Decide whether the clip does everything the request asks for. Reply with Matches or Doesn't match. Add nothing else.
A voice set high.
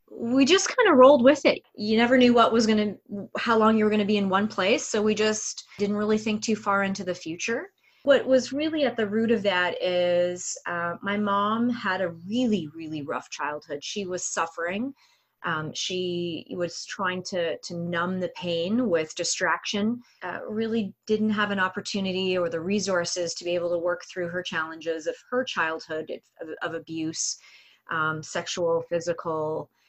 Matches